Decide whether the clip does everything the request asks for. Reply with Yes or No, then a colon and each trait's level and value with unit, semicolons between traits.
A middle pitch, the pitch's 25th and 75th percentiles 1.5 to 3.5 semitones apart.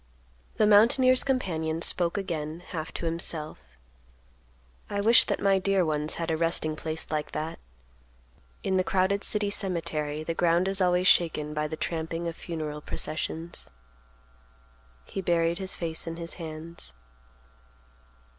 Yes: medium, 170 Hz; average, 2.9 semitones